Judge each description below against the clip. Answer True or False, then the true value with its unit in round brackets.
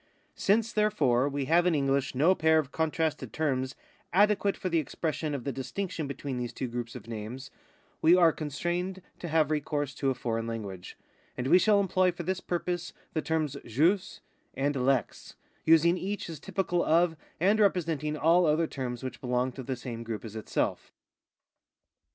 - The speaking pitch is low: False (155 Hz)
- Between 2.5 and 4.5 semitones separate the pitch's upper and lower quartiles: False (5.2 semitones)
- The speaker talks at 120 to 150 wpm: False (175 wpm)